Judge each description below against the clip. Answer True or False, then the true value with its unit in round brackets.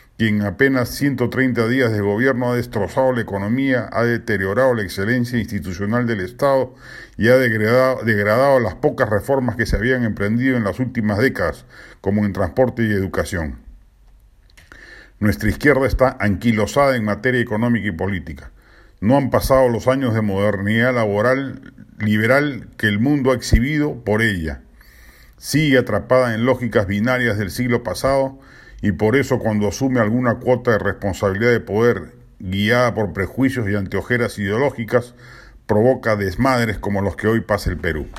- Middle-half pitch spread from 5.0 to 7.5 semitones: False (3.8 semitones)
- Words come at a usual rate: True (150 wpm)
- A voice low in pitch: True (115 Hz)